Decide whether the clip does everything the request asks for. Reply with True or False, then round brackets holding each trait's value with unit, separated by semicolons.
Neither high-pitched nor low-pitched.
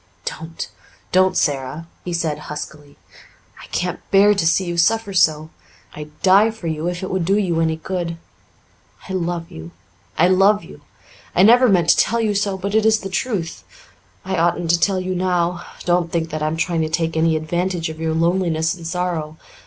True (175 Hz)